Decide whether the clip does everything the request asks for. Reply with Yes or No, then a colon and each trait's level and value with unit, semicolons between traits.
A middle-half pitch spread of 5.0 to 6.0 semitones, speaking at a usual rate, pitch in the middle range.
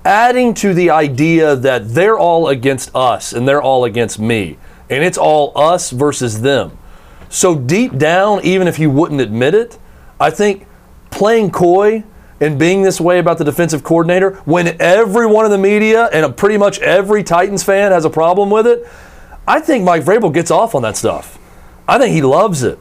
Yes: wide, 5.6 semitones; average, 185 wpm; medium, 175 Hz